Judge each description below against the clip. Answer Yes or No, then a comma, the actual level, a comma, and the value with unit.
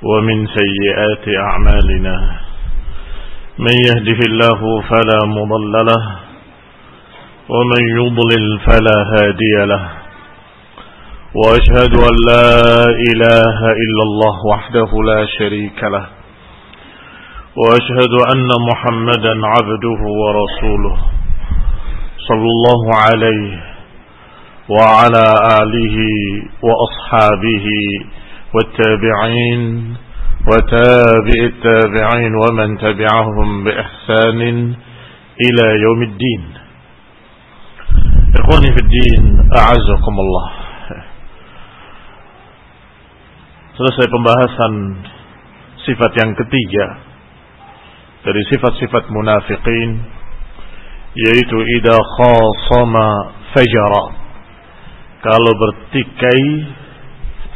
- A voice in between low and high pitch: No, low, 110 Hz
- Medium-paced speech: No, slow, 65 wpm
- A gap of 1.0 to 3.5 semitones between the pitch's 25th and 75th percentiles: Yes, narrow, 2.4 semitones